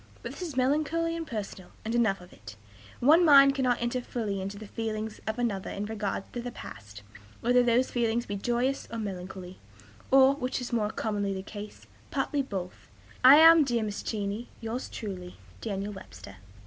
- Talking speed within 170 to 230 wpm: Yes, average, 180 wpm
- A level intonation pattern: No, average, 4.2 semitones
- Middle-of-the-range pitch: No, high, 225 Hz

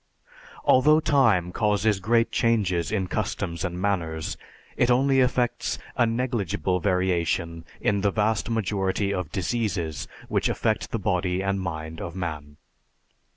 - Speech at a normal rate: No, slow, 130 wpm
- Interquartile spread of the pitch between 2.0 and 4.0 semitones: No, average, 4.7 semitones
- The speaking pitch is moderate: No, very low, 95 Hz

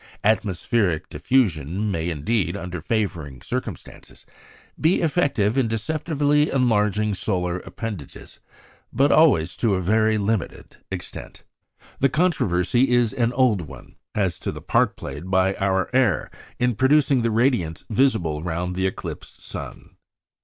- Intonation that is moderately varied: No, wide, 5.9 semitones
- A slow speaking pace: Yes, slow, 130 wpm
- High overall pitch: No, low, 105 Hz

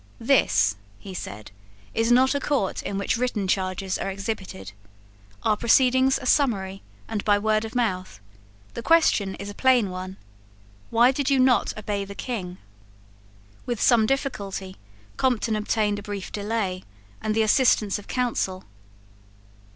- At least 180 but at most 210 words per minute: No, average, 145 wpm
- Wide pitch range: No, average, 4.2 semitones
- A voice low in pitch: No, high, 215 Hz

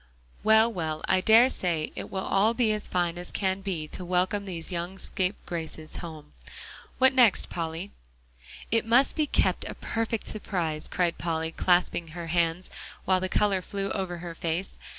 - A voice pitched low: No, medium, 185 Hz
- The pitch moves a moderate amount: Yes, average, 3.5 semitones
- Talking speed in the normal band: Yes, average, 170 wpm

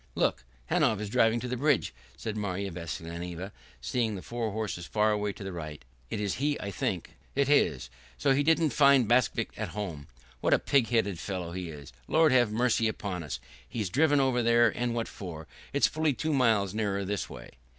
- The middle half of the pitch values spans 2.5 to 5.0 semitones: No, wide, 5.4 semitones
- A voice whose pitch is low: Yes, low, 110 Hz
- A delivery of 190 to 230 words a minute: Yes, average, 200 wpm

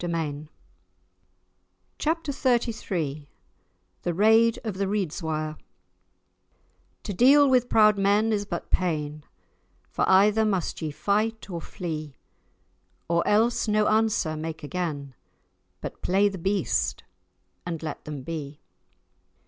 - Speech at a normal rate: No, slow, 110 wpm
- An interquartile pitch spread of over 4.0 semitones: Yes, wide, 5.6 semitones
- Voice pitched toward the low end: No, high, 195 Hz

